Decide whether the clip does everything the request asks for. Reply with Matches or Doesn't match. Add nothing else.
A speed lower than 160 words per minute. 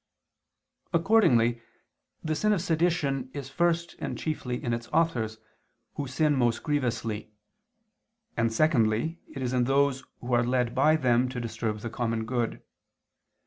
Matches